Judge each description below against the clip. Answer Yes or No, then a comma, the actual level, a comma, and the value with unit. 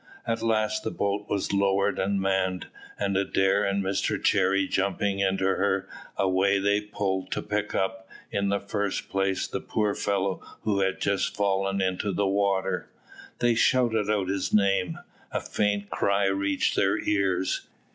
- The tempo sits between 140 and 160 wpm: Yes, average, 155 wpm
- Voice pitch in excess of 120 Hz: No, low, 100 Hz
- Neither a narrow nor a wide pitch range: No, narrow, 1.1 semitones